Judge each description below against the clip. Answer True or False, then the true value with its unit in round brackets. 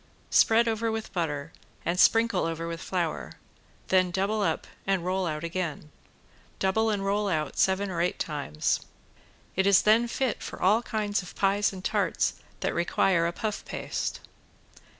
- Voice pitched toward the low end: False (190 Hz)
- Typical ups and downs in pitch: True (3.7 semitones)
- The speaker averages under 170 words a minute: True (160 wpm)